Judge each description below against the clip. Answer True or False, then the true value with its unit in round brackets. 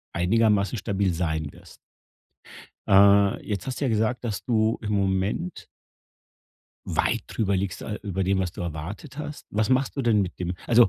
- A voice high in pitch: False (100 Hz)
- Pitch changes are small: False (3.2 semitones)